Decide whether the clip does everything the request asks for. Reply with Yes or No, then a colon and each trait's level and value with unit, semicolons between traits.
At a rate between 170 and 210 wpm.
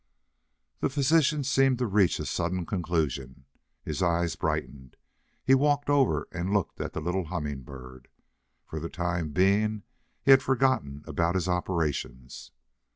No: average, 140 wpm